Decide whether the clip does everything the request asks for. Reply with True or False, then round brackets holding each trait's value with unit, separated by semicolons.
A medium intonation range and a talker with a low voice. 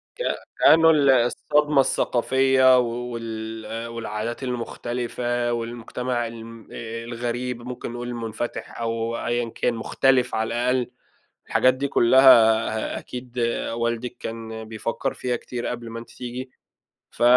False (1.5 semitones; 120 Hz)